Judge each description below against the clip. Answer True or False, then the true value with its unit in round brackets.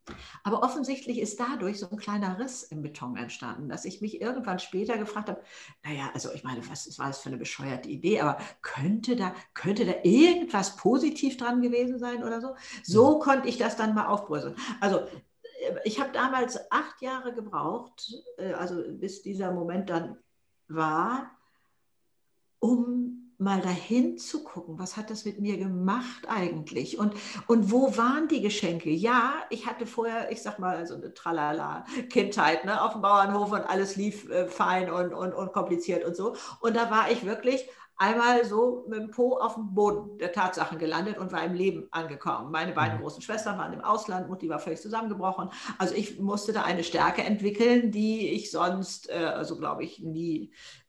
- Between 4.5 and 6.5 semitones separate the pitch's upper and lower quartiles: True (4.8 semitones)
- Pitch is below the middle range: False (210 Hz)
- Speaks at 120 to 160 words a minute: False (180 wpm)